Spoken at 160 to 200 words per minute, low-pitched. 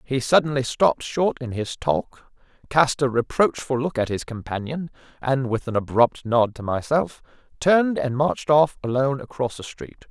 Yes: average, 170 wpm; low, 130 Hz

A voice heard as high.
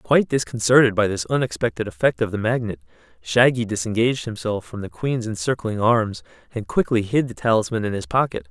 No: low, 110 Hz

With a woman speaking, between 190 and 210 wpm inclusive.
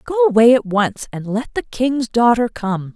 Yes: female; fast, 205 wpm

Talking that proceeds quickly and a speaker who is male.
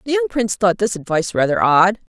No: fast, 220 wpm; female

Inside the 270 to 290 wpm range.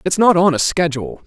No: fast, 235 wpm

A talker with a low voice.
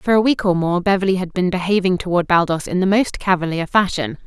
No: medium, 185 Hz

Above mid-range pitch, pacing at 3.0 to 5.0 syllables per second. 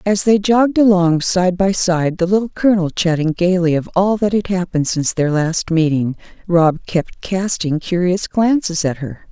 No: medium, 180 Hz; 4.8 syllables/s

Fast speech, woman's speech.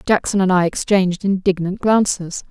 No: average, 145 wpm; female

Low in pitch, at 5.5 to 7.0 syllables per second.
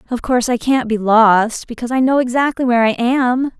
No: high, 240 Hz; 5.7 syllables/s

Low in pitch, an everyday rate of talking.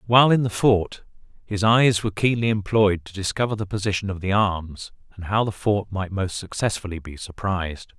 Yes: low, 100 Hz; average, 190 wpm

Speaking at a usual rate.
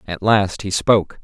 Yes: average, 195 wpm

